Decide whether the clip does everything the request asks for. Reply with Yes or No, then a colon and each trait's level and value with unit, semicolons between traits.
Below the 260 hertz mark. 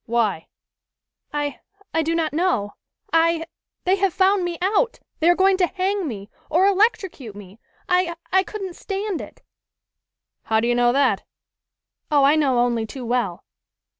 No: very high, 325 Hz